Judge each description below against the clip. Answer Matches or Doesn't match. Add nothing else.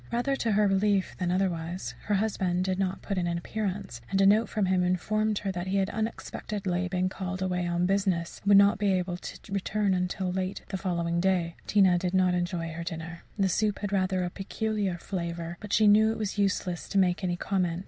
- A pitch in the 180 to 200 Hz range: Matches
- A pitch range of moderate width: Doesn't match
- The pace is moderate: Doesn't match